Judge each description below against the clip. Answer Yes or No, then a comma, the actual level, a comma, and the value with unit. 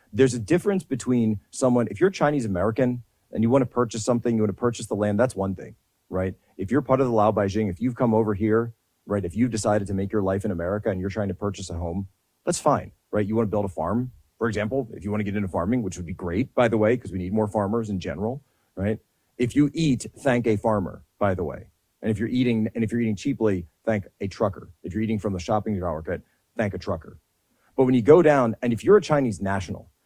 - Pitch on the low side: Yes, low, 110 Hz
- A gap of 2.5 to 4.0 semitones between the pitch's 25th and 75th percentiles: Yes, average, 3.6 semitones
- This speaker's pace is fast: Yes, fast, 260 wpm